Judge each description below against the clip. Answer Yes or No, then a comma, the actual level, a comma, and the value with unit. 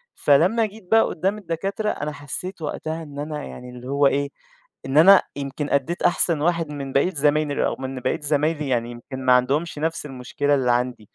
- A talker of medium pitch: Yes, medium, 145 Hz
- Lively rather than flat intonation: No, average, 3.7 semitones